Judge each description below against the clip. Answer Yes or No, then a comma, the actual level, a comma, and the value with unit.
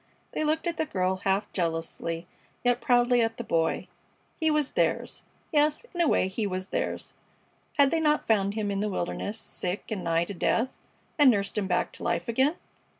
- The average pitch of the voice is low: No, high, 215 Hz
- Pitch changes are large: Yes, wide, 7.2 semitones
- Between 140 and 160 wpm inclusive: No, average, 195 wpm